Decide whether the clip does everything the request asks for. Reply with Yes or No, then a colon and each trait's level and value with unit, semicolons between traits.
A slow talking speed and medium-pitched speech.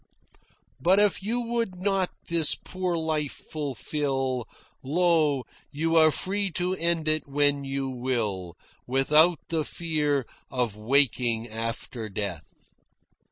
Yes: slow, 115 wpm; medium, 145 Hz